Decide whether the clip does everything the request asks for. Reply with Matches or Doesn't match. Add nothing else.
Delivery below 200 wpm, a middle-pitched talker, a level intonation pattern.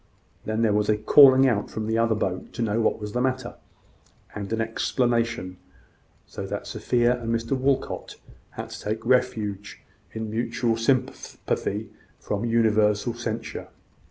Doesn't match